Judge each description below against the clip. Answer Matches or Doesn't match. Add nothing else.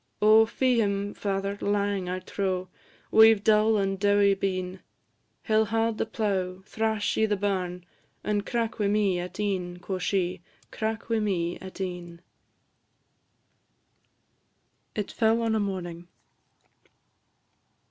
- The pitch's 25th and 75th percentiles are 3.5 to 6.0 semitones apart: Doesn't match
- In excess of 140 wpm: Doesn't match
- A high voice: Matches